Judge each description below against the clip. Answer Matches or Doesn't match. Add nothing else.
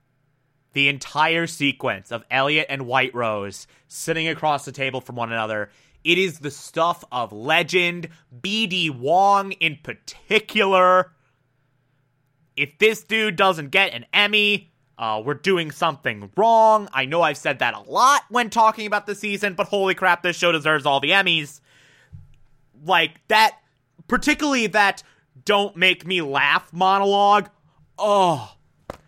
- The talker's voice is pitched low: Doesn't match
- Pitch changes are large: Matches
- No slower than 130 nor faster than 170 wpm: Matches